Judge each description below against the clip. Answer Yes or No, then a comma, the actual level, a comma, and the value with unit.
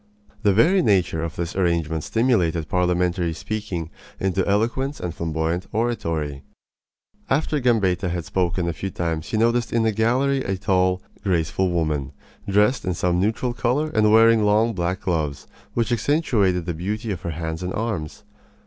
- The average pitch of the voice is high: No, very low, 95 Hz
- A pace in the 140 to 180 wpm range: Yes, average, 160 wpm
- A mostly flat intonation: No, average, 5.0 semitones